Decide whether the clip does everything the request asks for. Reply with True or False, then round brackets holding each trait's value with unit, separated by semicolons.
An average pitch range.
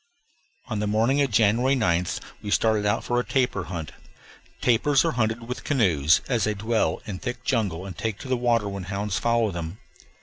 True (3.7 semitones)